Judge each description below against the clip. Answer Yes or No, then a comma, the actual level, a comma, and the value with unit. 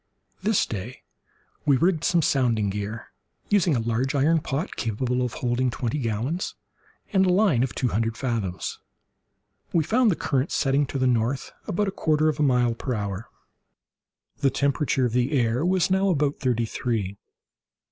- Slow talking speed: No, average, 165 wpm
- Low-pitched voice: Yes, low, 130 Hz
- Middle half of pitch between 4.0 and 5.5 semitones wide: Yes, average, 5.1 semitones